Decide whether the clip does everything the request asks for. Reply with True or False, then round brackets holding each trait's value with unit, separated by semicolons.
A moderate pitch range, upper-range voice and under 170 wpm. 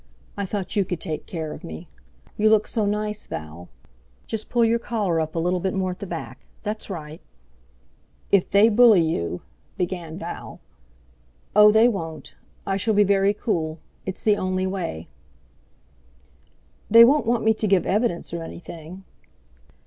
True (4.3 semitones; 195 Hz; 160 wpm)